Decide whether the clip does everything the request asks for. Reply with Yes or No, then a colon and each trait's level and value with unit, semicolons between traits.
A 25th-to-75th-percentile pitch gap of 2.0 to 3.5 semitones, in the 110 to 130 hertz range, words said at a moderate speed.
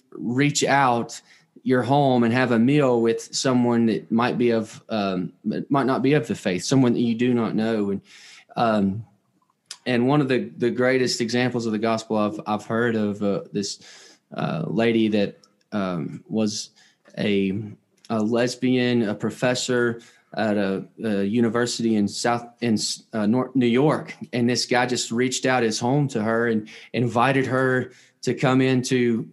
Yes: narrow, 2.4 semitones; low, 120 Hz; average, 170 wpm